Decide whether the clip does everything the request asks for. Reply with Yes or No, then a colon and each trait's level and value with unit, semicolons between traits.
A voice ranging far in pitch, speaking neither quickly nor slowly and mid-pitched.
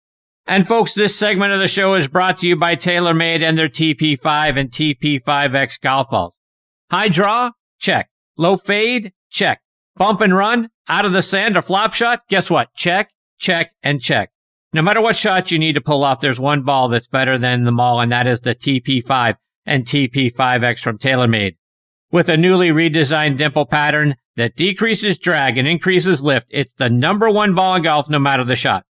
Yes: wide, 5.7 semitones; average, 190 wpm; medium, 155 Hz